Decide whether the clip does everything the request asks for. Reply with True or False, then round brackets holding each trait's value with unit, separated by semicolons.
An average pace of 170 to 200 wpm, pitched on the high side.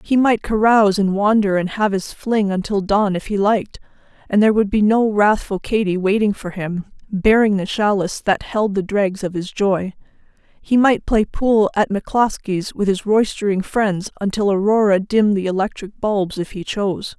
True (185 wpm; 205 Hz)